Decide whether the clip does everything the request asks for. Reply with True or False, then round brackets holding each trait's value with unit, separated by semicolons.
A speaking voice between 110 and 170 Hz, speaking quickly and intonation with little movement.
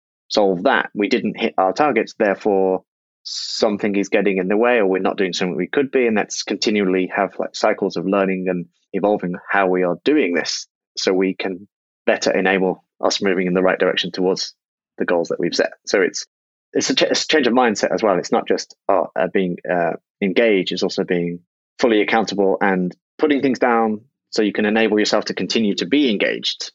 False (95 Hz; 210 wpm; 1.9 semitones)